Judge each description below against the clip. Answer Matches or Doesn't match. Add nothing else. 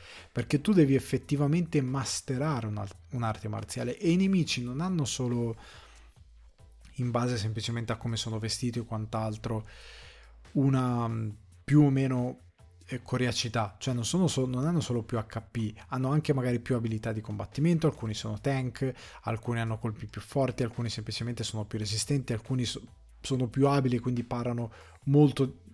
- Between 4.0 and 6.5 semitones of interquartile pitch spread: Doesn't match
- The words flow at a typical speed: Matches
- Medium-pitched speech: Doesn't match